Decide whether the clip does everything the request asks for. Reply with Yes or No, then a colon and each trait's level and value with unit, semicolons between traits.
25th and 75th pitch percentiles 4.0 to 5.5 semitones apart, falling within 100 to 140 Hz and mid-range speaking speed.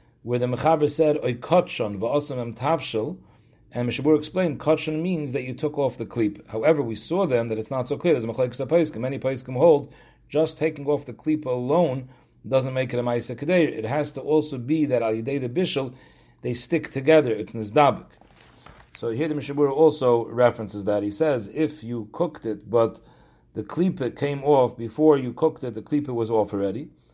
Yes: average, 4.8 semitones; low, 135 Hz; average, 180 wpm